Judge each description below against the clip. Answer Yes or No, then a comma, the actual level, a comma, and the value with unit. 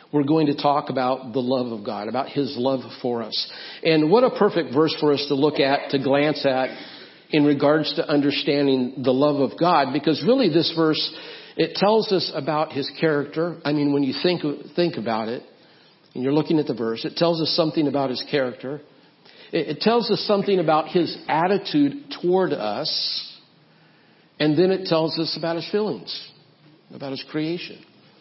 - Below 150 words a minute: No, average, 185 wpm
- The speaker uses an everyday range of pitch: Yes, average, 3.3 semitones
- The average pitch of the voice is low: No, medium, 150 Hz